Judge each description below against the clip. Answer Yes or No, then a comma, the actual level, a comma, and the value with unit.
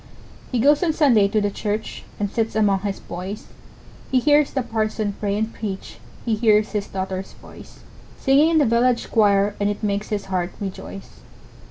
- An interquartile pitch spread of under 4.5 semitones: Yes, average, 2.9 semitones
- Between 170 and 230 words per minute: Yes, average, 180 wpm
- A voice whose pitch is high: Yes, high, 210 Hz